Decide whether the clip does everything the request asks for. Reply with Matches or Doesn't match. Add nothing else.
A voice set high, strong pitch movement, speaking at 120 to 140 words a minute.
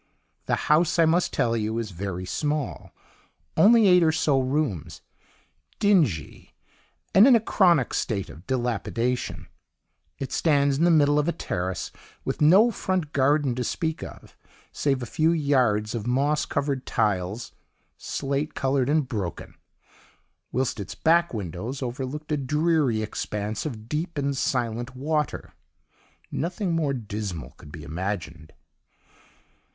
Doesn't match